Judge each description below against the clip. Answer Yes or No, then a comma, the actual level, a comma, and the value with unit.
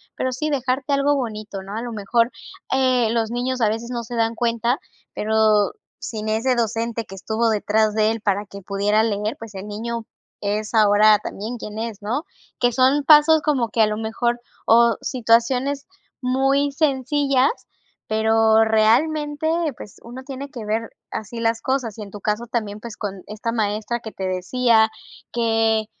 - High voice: Yes, high, 230 Hz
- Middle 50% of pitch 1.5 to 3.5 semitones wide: Yes, average, 2.8 semitones